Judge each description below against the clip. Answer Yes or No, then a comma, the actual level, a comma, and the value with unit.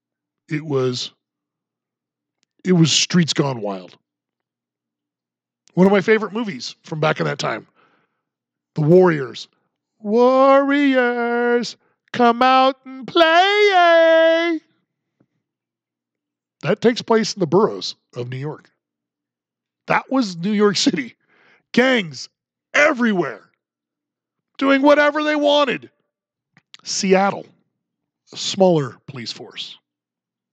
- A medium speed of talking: No, slow, 95 wpm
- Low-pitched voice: No, high, 190 Hz